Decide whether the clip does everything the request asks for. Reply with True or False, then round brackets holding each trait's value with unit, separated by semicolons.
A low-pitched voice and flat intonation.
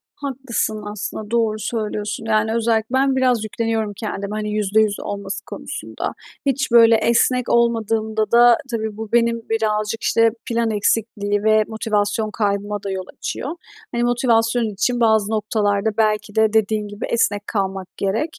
False (220 Hz; 1.8 semitones)